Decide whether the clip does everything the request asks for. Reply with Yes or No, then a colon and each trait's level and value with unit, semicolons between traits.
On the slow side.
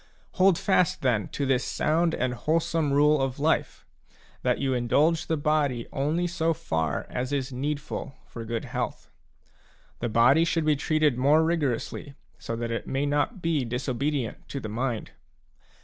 No: average, 165 wpm